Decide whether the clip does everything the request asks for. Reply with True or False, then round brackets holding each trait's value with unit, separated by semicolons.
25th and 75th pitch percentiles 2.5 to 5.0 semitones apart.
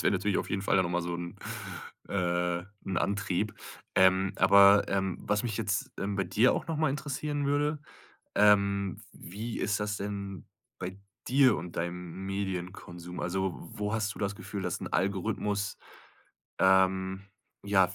False (1.8 semitones)